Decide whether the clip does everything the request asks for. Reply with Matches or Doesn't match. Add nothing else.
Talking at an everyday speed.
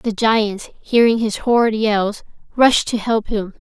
Matches